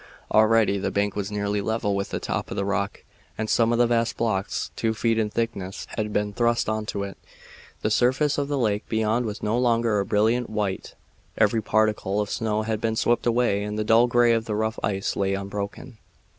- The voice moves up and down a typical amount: No, narrow, 2.2 semitones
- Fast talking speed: Yes, fast, 210 wpm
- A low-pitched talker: Yes, low, 110 Hz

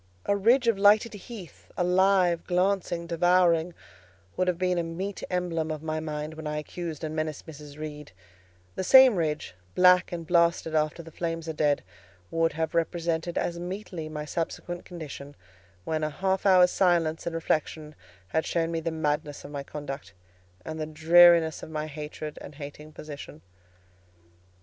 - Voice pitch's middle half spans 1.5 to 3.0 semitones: Yes, narrow, 2.6 semitones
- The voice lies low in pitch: No, medium, 165 Hz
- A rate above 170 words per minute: No, average, 165 wpm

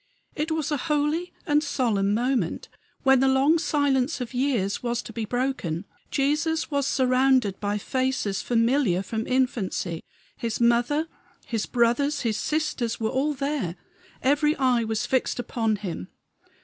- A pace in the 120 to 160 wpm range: Yes, average, 145 wpm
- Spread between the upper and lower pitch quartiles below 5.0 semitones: Yes, average, 4.2 semitones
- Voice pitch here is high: Yes, very high, 255 Hz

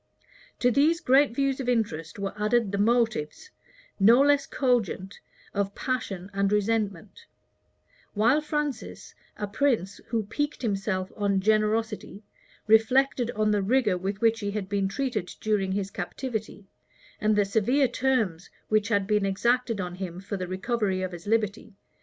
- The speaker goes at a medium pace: Yes, average, 150 wpm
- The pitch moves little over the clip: No, average, 3.6 semitones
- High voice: Yes, high, 215 Hz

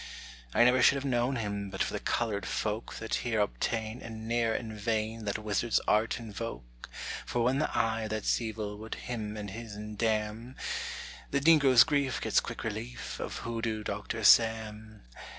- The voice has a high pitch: No, low, 110 Hz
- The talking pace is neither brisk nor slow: Yes, average, 170 wpm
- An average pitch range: No, narrow, 1.9 semitones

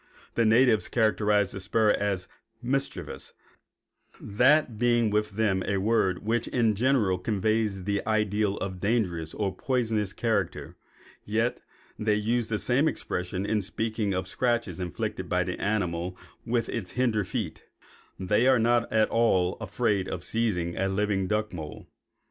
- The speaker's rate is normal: Yes, average, 150 wpm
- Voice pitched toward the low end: Yes, low, 105 Hz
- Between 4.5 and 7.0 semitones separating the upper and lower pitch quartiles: No, average, 3.2 semitones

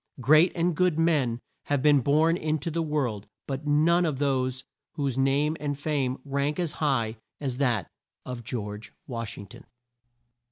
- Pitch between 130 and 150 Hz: Yes, medium, 140 Hz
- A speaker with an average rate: Yes, average, 155 wpm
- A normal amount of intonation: Yes, average, 3.3 semitones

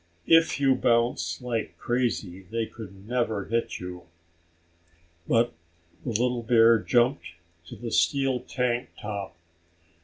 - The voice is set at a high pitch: No, low, 115 Hz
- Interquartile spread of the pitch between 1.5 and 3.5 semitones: Yes, narrow, 2.6 semitones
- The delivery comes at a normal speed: No, slow, 120 wpm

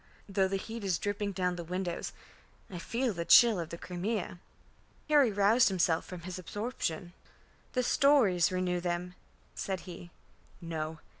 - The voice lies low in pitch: No, medium, 185 Hz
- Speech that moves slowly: No, average, 150 wpm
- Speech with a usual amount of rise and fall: Yes, average, 3.1 semitones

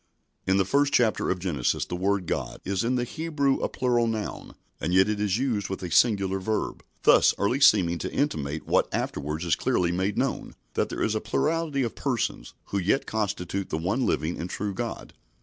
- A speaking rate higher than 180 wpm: Yes, average, 200 wpm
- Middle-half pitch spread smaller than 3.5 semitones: No, average, 5.1 semitones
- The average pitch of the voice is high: No, low, 100 Hz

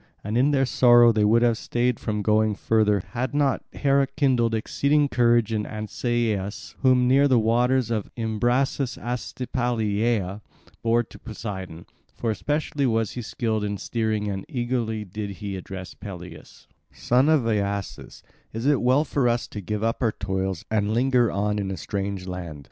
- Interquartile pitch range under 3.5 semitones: Yes, average, 3.1 semitones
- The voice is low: Yes, low, 115 Hz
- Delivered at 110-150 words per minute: No, average, 165 wpm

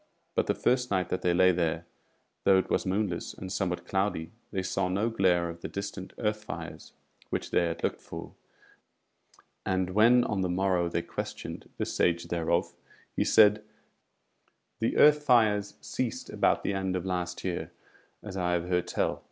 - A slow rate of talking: No, average, 175 wpm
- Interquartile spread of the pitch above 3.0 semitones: No, average, 2.7 semitones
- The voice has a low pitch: Yes, very low, 95 Hz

